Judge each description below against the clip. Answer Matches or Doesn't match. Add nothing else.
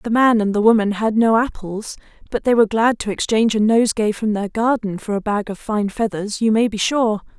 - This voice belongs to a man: Doesn't match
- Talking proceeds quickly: Matches